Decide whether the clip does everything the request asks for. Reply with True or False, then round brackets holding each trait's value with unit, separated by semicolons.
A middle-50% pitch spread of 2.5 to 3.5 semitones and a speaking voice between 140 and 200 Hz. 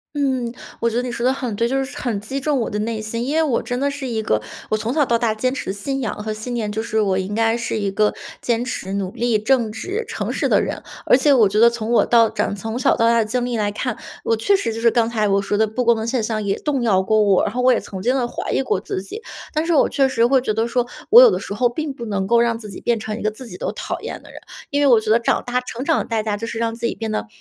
False (2.8 semitones; 230 Hz)